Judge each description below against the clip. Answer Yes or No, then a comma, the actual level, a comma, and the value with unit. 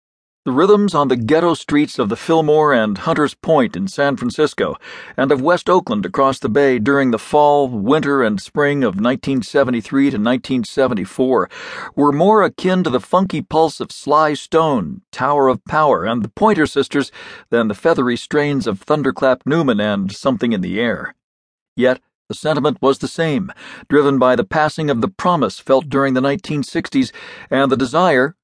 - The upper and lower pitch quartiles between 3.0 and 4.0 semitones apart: Yes, average, 3.4 semitones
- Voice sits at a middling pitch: Yes, medium, 145 Hz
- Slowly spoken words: No, average, 170 wpm